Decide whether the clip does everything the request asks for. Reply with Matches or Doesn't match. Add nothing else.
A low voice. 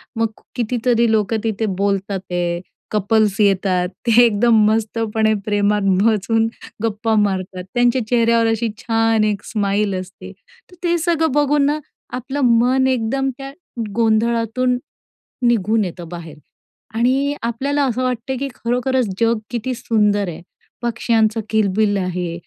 Doesn't match